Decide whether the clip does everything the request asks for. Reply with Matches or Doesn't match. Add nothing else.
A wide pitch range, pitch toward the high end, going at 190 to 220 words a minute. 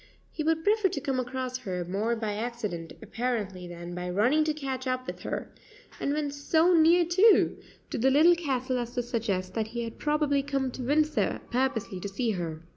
Matches